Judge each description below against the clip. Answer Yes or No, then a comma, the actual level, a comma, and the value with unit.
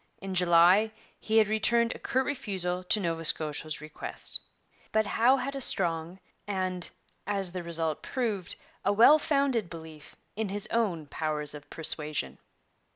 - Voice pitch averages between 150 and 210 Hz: Yes, medium, 185 Hz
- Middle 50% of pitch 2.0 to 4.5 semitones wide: No, average, 5.2 semitones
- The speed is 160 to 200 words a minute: No, average, 150 wpm